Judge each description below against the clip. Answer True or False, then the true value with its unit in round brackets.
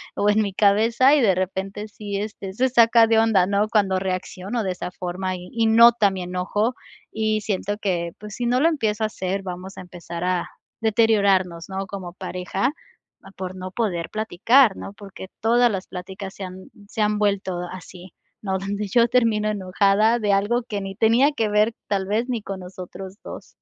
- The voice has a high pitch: True (200 Hz)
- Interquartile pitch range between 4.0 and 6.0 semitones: False (2.9 semitones)